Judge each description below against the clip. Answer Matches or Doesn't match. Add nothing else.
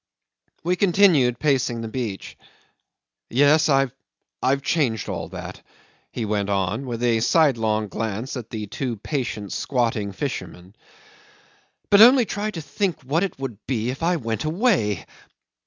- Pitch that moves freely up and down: Matches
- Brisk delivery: Doesn't match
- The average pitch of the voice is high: Doesn't match